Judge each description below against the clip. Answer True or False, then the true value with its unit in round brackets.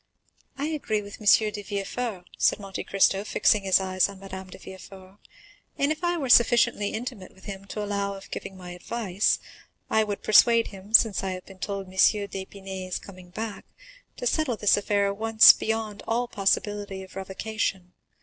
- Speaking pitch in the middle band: False (200 Hz)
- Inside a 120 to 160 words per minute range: False (180 wpm)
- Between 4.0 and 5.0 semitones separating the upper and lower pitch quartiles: False (2.5 semitones)